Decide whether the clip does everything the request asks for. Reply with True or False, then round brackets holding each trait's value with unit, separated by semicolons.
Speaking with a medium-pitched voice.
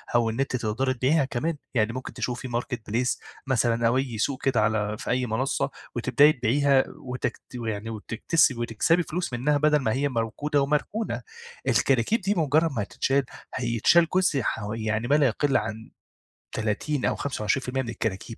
False (125 Hz)